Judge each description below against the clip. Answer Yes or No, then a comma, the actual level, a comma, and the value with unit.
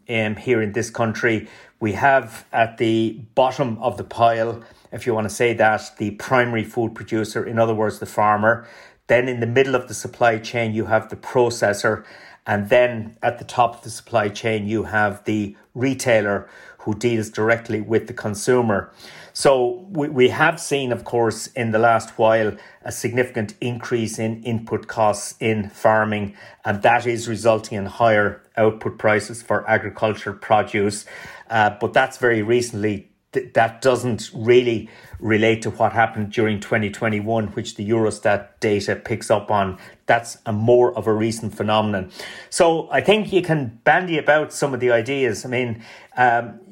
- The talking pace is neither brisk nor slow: Yes, average, 165 wpm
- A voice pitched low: Yes, low, 115 Hz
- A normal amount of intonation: No, narrow, 2.0 semitones